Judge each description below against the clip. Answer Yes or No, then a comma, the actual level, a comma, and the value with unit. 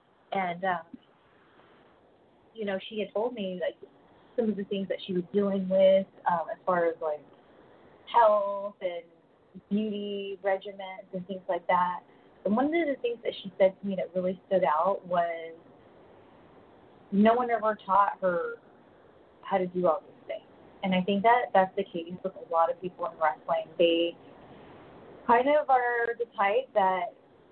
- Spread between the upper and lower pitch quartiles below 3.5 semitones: Yes, average, 2.9 semitones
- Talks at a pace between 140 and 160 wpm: No, average, 170 wpm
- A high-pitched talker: Yes, high, 195 Hz